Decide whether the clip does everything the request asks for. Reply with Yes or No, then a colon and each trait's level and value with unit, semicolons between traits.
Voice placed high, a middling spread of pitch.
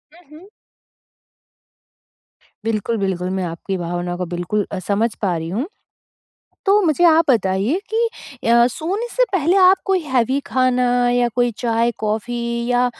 No: high, 235 Hz; wide, 7.9 semitones